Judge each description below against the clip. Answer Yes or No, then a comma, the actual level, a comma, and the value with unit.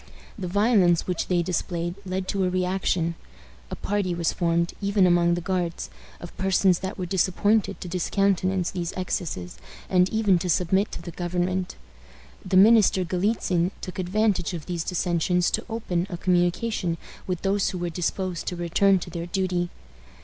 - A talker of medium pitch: Yes, medium, 180 Hz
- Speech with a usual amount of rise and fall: No, narrow, 1.8 semitones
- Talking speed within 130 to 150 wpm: No, average, 165 wpm